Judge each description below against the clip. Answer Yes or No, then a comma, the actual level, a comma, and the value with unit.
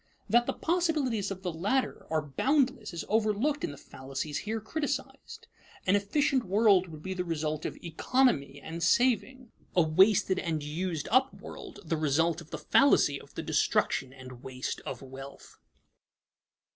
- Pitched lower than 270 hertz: Yes, medium, 185 Hz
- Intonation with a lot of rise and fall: Yes, wide, 8.2 semitones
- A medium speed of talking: Yes, average, 160 wpm